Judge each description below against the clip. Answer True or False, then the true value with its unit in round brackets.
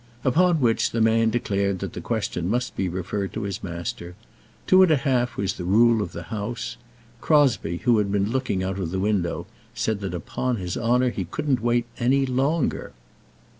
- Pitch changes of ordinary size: True (4.9 semitones)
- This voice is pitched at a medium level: False (110 Hz)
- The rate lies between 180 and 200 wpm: True (185 wpm)